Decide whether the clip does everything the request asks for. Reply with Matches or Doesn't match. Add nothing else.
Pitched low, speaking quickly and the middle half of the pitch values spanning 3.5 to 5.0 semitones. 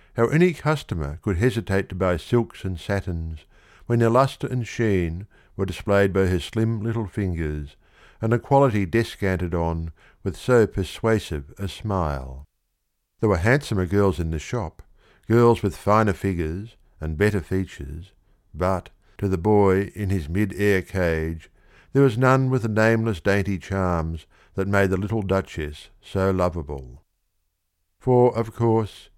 Doesn't match